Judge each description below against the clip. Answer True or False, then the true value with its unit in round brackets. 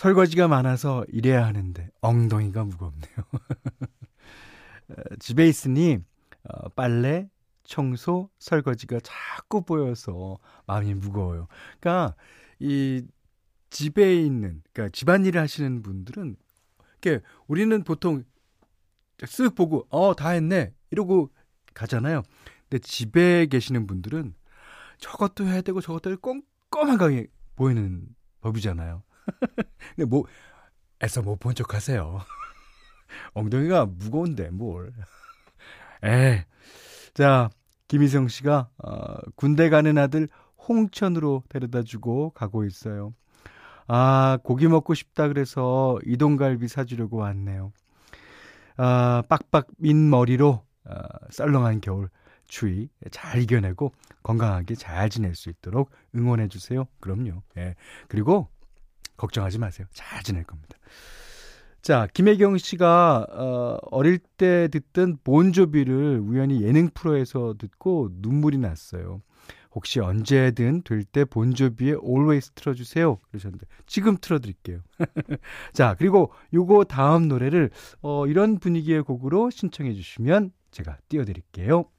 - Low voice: True (130 Hz)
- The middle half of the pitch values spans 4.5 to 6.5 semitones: False (6.9 semitones)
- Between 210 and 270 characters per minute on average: True (255 characters per minute)